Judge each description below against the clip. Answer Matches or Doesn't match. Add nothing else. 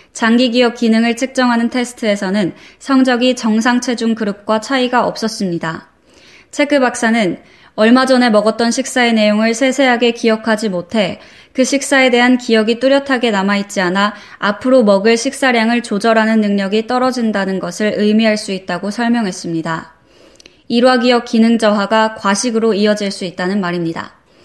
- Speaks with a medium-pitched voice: Doesn't match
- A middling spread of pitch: Matches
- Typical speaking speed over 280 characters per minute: Matches